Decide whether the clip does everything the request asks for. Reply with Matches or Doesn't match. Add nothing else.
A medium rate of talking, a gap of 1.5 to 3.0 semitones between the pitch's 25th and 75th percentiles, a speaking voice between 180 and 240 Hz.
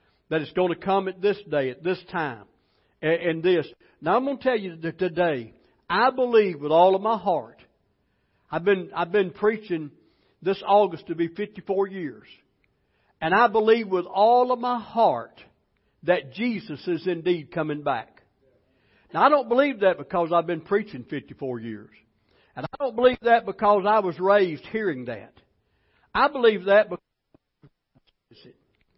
Doesn't match